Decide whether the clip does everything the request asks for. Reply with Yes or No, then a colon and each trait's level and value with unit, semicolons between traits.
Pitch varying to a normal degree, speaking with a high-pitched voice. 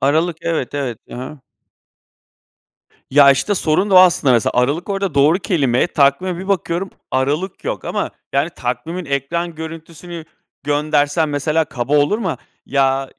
No: average, 3.8 semitones; medium, 155 Hz